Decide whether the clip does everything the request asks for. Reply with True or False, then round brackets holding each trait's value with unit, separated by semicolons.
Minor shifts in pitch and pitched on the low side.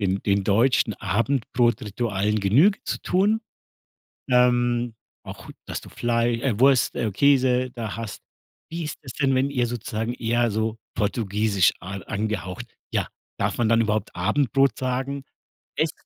False (3.3 semitones; 120 Hz)